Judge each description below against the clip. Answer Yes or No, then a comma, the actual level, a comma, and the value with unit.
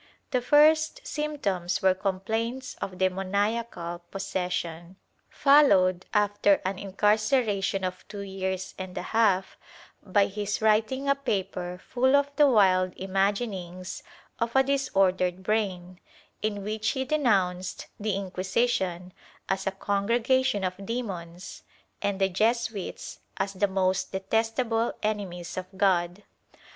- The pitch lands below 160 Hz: No, high, 200 Hz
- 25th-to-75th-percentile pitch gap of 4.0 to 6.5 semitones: No, average, 3.5 semitones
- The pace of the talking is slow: Yes, slow, 120 wpm